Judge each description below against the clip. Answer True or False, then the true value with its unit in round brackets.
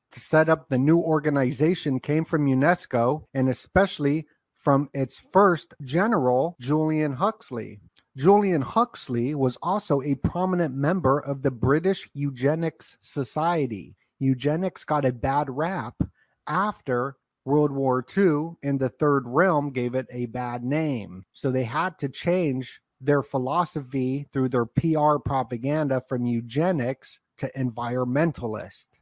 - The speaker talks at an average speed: False (125 wpm)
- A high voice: False (140 Hz)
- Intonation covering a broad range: False (3.5 semitones)